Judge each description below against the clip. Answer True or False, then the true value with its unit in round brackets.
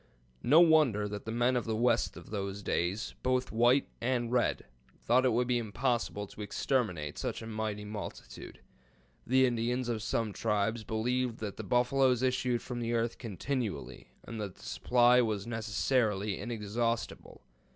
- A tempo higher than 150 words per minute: True (160 wpm)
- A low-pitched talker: True (115 Hz)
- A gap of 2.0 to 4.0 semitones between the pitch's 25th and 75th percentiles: True (2.7 semitones)